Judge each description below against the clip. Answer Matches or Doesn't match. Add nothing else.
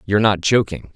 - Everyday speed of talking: Matches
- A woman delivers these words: Doesn't match